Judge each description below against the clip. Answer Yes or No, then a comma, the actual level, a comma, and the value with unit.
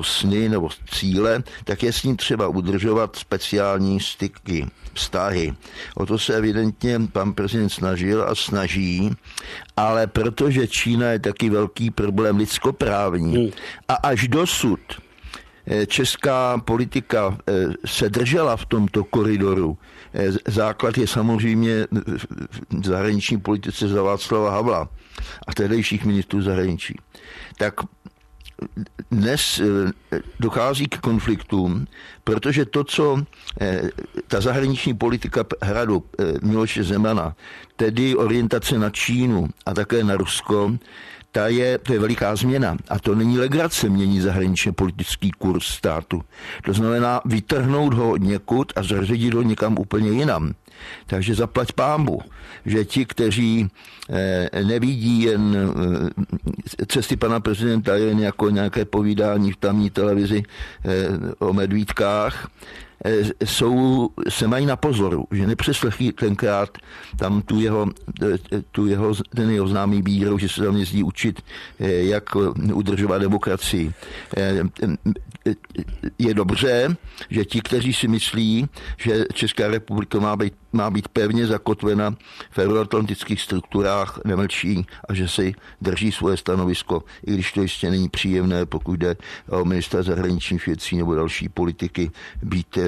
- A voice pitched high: No, low, 105 Hz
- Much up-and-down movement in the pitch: No, average, 2.9 semitones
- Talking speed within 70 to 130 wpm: Yes, average, 120 wpm